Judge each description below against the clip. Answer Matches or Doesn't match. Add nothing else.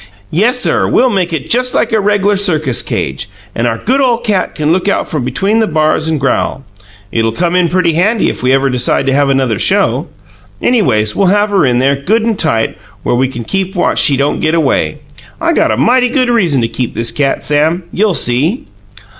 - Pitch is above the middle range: Doesn't match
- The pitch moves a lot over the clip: Matches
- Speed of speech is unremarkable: Doesn't match